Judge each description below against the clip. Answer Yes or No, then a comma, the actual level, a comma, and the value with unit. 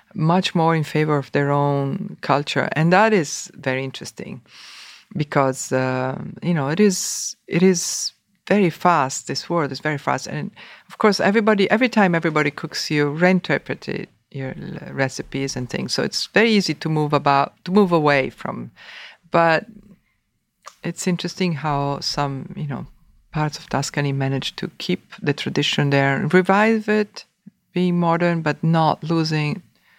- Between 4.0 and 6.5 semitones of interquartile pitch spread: Yes, average, 4.5 semitones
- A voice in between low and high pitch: Yes, medium, 160 Hz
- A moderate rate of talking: Yes, average, 155 wpm